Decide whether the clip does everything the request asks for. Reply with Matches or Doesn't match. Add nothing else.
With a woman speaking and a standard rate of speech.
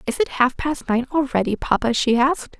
Doesn't match